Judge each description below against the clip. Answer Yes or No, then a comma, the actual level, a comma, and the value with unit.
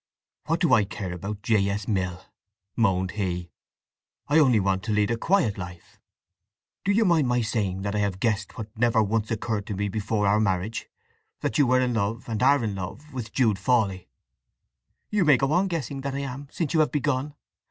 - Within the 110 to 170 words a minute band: No, average, 200 wpm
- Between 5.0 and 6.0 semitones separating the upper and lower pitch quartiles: Yes, average, 5.3 semitones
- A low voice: Yes, low, 110 Hz